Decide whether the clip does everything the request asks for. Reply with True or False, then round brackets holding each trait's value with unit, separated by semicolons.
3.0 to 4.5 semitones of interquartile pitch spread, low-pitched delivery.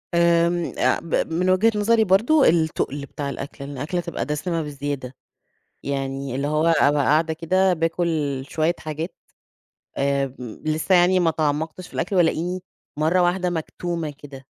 False (3.5 semitones; 160 Hz)